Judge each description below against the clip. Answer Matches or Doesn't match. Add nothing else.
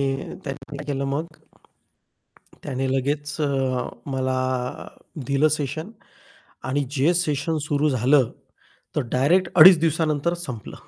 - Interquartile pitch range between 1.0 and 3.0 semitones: Matches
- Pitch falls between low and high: Matches